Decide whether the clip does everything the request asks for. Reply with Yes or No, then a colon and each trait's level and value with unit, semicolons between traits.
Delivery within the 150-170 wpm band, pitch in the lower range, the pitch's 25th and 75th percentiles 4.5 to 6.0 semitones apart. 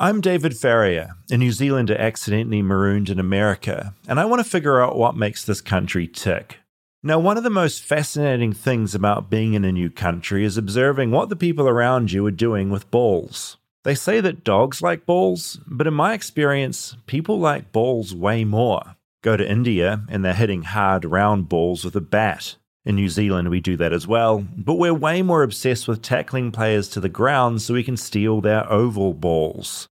No: average, 195 wpm; low, 110 Hz; average, 5.2 semitones